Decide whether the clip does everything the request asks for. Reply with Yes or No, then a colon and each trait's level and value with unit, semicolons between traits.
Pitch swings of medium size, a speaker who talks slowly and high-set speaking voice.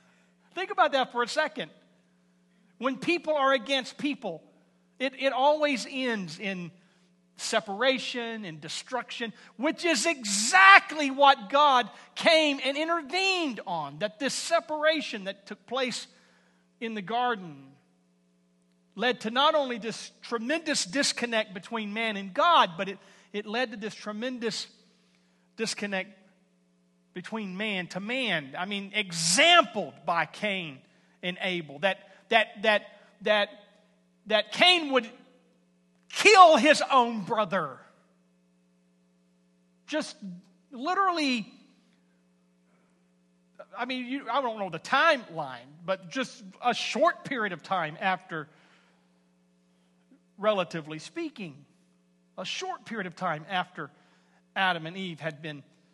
No: wide, 8.3 semitones; slow, 115 wpm; high, 205 Hz